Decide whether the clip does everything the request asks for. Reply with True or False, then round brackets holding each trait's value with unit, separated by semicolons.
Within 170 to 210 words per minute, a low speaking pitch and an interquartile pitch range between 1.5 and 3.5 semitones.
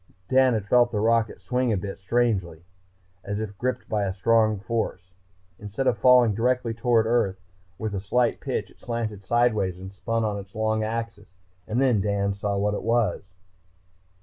True (180 wpm; 110 Hz; 2.9 semitones)